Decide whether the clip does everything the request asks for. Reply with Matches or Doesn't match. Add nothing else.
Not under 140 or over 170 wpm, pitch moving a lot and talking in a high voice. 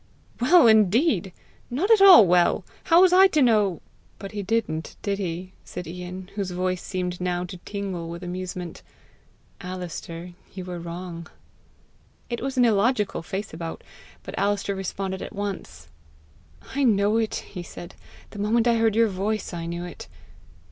Doesn't match